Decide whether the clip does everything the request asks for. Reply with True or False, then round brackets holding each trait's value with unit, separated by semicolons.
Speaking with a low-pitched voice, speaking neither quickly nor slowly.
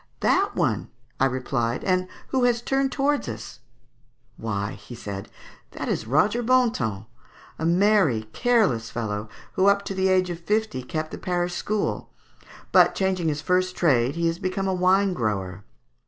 False (175 Hz; 160 wpm)